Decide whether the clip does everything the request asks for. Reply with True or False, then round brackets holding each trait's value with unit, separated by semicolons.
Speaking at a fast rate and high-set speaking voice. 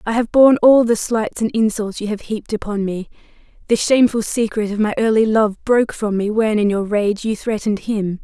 True (220 wpm; 215 Hz)